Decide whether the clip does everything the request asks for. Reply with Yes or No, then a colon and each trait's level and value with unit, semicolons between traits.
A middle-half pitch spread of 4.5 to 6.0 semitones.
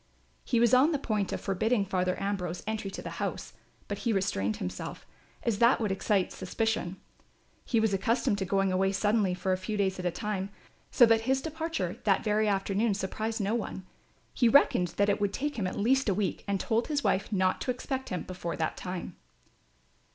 No: average, 3.4 semitones